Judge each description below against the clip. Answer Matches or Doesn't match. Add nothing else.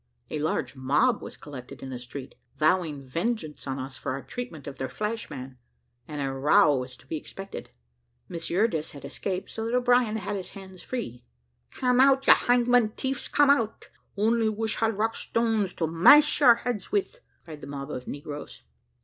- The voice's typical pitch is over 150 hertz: Matches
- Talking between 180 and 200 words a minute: Matches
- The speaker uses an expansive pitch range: Matches